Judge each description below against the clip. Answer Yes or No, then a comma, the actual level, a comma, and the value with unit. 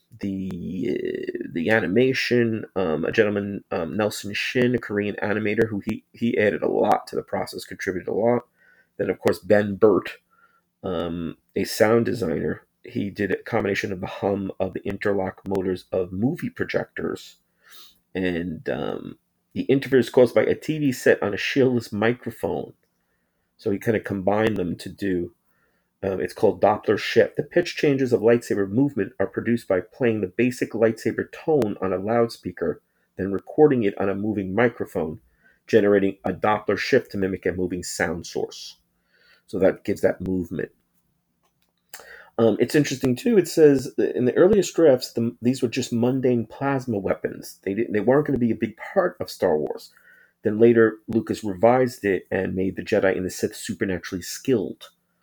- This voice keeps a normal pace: Yes, average, 170 wpm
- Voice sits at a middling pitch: No, low, 115 Hz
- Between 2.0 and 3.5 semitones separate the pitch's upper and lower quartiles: No, average, 4.3 semitones